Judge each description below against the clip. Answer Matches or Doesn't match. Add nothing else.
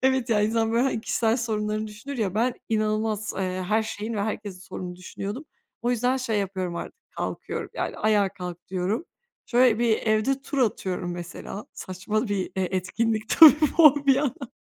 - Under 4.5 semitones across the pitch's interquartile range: Matches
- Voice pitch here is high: Matches